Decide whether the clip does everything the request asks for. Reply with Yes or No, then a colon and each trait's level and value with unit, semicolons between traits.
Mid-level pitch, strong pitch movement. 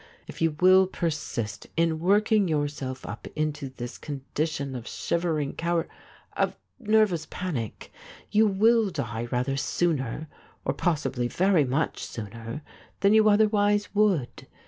Yes: medium, 160 Hz; wide, 6.5 semitones